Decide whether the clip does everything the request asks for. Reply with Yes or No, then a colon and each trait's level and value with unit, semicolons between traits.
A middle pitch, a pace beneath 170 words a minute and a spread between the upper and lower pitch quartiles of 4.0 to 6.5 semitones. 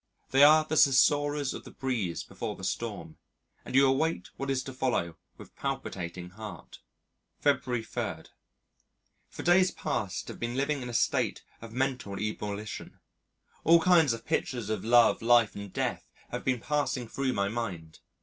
No: low, 120 Hz; average, 160 wpm; average, 4.7 semitones